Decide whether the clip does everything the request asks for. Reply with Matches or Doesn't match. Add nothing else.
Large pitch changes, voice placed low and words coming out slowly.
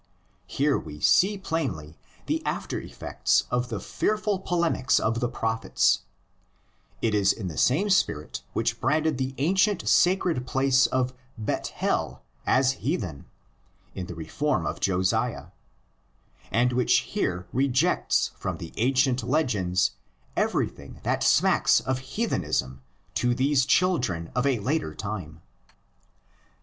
Matches